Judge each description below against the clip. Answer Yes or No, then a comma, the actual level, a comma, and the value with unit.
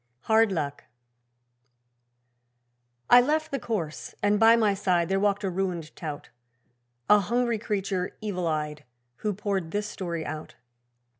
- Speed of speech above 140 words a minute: No, slow, 135 wpm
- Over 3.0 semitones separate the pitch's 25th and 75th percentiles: Yes, average, 4.1 semitones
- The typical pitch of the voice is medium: No, high, 195 Hz